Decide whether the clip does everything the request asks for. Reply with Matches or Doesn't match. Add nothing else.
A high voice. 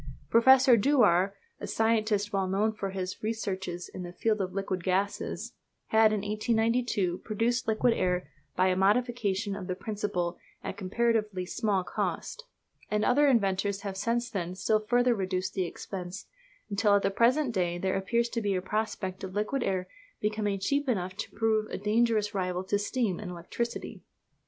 Matches